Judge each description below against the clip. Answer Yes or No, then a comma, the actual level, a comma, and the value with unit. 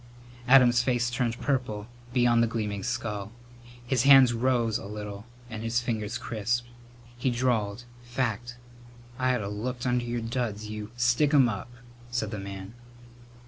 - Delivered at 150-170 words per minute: Yes, average, 155 wpm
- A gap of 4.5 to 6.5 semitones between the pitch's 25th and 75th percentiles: No, narrow, 2.4 semitones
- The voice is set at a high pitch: No, low, 120 Hz